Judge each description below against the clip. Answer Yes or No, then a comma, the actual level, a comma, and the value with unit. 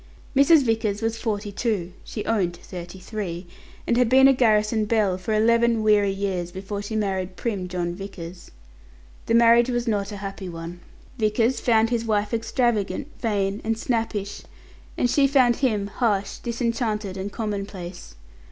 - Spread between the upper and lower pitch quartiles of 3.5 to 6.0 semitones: No, average, 3.0 semitones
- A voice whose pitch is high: Yes, high, 210 Hz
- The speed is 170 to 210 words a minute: No, average, 160 wpm